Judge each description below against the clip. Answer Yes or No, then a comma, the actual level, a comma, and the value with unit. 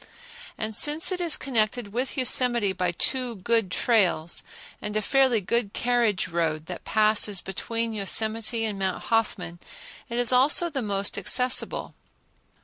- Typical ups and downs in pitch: Yes, average, 3.9 semitones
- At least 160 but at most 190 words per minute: No, average, 145 wpm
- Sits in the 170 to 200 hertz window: No, high, 225 Hz